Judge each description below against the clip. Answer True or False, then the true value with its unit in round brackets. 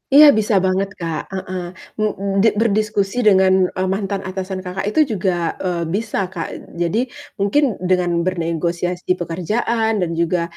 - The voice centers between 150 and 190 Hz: True (185 Hz)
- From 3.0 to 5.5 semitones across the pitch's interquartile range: False (2.6 semitones)